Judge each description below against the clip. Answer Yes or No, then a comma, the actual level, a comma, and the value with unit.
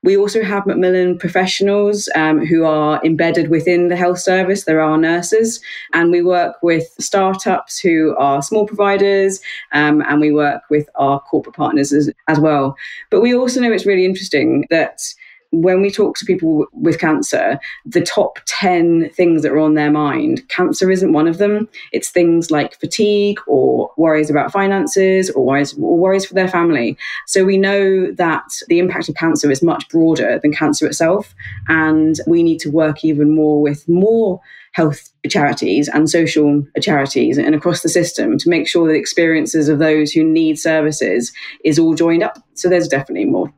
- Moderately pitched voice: Yes, medium, 165 Hz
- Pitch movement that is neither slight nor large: Yes, average, 3.7 semitones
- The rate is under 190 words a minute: Yes, average, 180 wpm